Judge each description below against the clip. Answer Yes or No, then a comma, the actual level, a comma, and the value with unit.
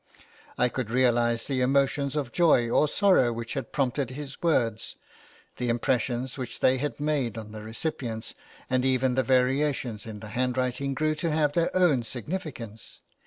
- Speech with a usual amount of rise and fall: Yes, average, 3.5 semitones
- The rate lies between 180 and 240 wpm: No, average, 165 wpm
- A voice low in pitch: Yes, low, 130 Hz